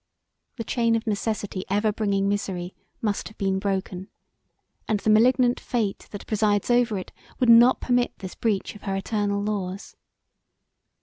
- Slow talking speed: No, average, 150 wpm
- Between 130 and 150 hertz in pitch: No, high, 210 Hz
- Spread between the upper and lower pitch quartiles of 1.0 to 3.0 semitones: Yes, narrow, 2.6 semitones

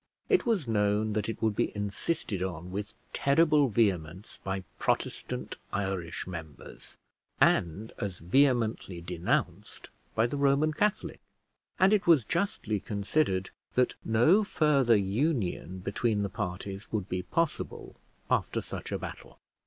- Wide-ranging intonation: Yes, wide, 6.7 semitones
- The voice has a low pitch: Yes, low, 105 Hz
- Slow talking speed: Yes, slow, 130 wpm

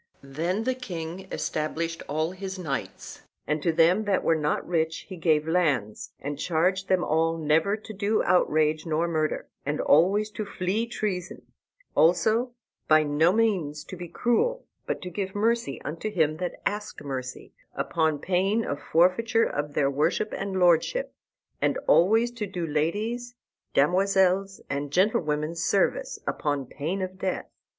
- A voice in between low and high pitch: Yes, medium, 175 Hz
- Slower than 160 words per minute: Yes, average, 150 wpm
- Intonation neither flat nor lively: Yes, average, 4.5 semitones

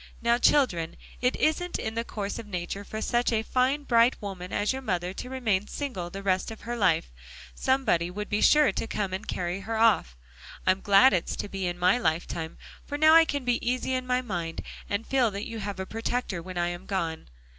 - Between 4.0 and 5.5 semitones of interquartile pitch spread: Yes, average, 5.2 semitones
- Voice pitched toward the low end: No, high, 210 Hz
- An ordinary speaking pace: No, fast, 220 wpm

